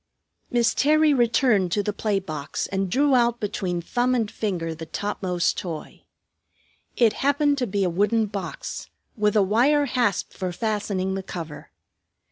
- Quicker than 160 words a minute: No, average, 155 wpm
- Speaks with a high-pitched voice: Yes, high, 210 Hz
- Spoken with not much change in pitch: No, average, 4.6 semitones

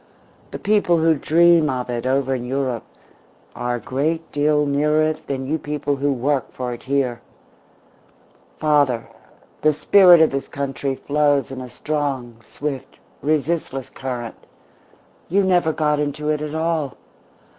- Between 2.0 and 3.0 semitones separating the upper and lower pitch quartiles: Yes, average, 2.7 semitones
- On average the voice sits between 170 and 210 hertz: No, medium, 145 Hz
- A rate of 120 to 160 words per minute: Yes, average, 145 wpm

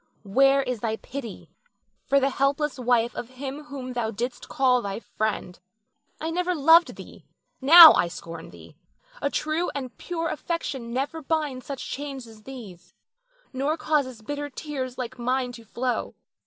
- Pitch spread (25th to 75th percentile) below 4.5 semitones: Yes, average, 3.5 semitones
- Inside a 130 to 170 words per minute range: Yes, average, 155 wpm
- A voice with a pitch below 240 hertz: No, very high, 260 Hz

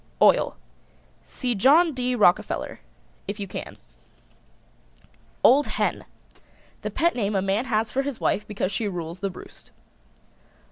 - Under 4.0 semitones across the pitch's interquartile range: No, average, 4.7 semitones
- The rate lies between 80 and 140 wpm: Yes, slow, 135 wpm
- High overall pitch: Yes, high, 215 Hz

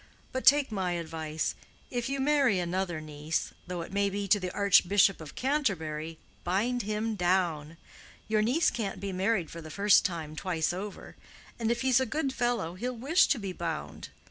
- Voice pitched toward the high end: Yes, high, 195 Hz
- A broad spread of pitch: Yes, wide, 5.8 semitones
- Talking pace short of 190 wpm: Yes, average, 180 wpm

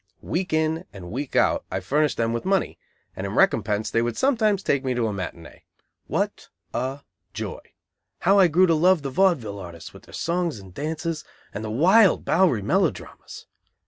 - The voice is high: No, medium, 150 Hz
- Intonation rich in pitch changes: Yes, wide, 7.9 semitones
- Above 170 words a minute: Yes, average, 180 wpm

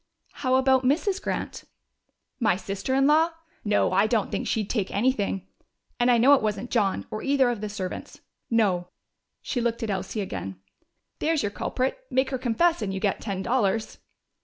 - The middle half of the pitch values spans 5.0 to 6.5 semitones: No, average, 4.6 semitones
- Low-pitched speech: No, high, 230 Hz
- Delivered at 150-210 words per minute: Yes, average, 180 wpm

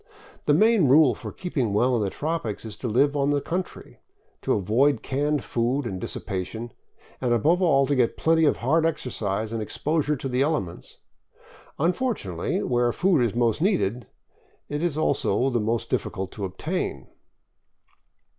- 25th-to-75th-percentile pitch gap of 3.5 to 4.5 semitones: No, wide, 5.5 semitones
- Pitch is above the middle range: No, low, 130 Hz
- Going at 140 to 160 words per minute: Yes, average, 155 wpm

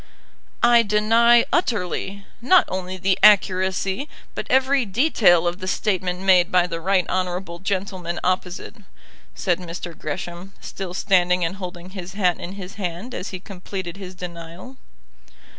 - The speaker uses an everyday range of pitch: No, narrow, 2.2 semitones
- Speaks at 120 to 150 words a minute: Yes, average, 140 wpm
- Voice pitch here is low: No, medium, 185 Hz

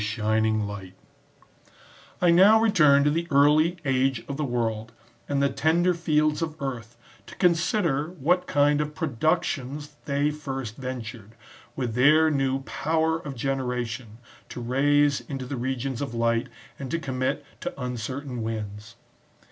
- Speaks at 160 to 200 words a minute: No, average, 140 wpm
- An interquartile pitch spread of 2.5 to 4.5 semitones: Yes, average, 4.1 semitones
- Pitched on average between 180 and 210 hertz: No, low, 135 Hz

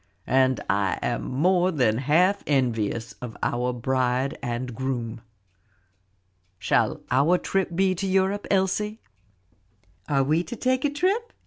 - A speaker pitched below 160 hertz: Yes, medium, 140 Hz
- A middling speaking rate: No, slow, 130 wpm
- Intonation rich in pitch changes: Yes, wide, 7.5 semitones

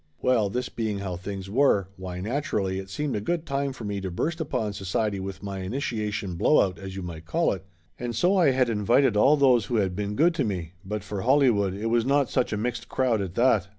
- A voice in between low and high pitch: No, low, 105 Hz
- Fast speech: Yes, fast, 230 wpm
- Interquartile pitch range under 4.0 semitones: No, average, 5.1 semitones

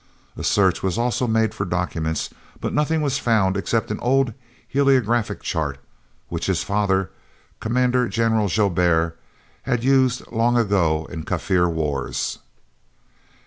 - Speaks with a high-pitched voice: No, low, 105 Hz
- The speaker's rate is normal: No, slow, 130 wpm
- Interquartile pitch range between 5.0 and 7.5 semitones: Yes, wide, 5.6 semitones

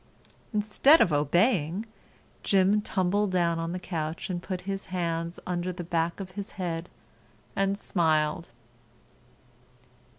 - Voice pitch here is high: No, medium, 180 Hz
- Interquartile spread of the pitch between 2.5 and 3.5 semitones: Yes, average, 2.8 semitones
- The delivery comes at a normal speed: No, slow, 125 wpm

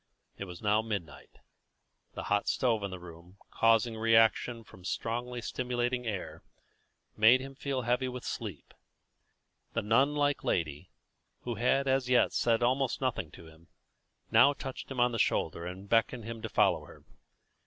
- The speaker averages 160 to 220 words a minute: Yes, average, 165 wpm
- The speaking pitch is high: No, low, 115 Hz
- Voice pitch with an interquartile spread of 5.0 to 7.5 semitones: No, average, 3.7 semitones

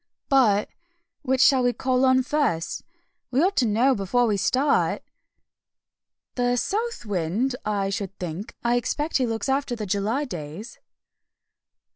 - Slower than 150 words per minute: Yes, average, 140 wpm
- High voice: Yes, high, 245 Hz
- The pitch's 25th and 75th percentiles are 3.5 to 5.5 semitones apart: Yes, average, 4.7 semitones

